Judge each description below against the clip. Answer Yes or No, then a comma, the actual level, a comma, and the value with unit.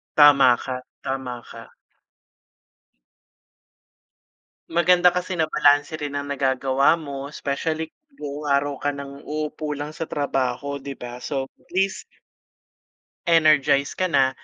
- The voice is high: No, medium, 145 Hz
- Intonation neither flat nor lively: No, narrow, 2.1 semitones